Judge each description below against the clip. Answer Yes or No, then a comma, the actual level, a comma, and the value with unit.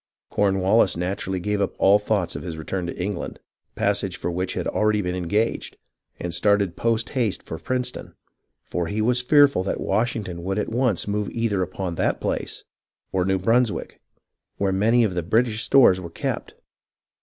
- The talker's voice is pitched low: Yes, low, 100 Hz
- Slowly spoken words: No, average, 170 wpm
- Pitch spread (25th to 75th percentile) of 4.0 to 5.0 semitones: No, average, 3.5 semitones